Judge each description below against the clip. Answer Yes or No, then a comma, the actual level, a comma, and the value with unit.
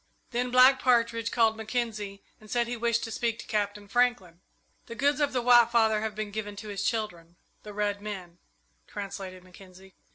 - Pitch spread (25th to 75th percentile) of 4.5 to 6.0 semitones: No, average, 2.9 semitones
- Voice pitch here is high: Yes, high, 215 Hz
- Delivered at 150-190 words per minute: Yes, average, 185 wpm